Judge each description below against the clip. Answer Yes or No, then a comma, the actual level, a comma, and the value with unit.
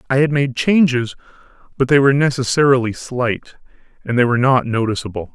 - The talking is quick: No, average, 155 wpm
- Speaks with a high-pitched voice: No, low, 130 Hz